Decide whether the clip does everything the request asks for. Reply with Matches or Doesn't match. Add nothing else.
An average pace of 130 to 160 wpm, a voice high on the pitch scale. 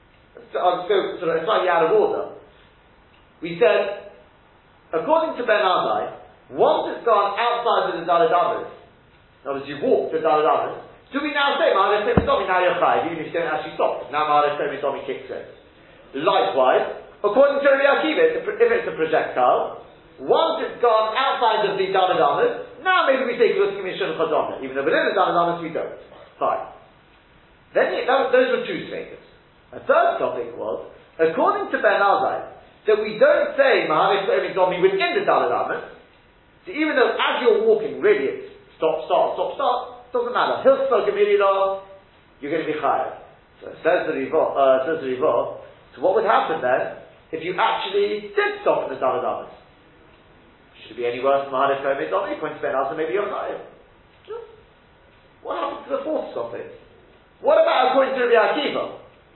Doesn't match